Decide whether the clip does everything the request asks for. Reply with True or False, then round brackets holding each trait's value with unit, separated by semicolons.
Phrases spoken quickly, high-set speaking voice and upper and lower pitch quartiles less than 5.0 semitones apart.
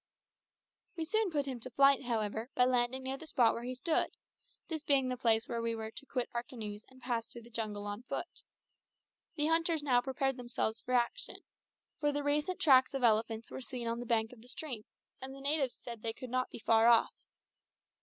True (215 wpm; 250 Hz; 3.0 semitones)